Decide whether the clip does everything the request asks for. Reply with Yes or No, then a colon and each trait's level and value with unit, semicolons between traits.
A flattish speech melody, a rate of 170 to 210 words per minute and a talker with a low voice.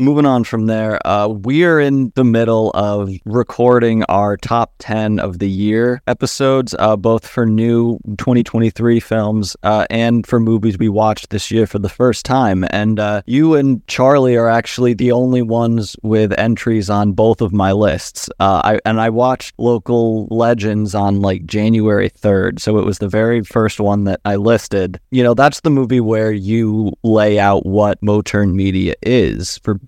Yes: narrow, 2.3 semitones; average, 180 wpm; low, 110 Hz